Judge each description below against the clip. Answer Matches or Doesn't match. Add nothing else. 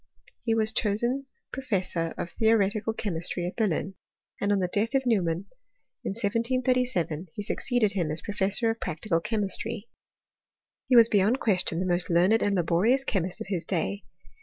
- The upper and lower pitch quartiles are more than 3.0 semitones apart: Matches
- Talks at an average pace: Matches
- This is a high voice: Matches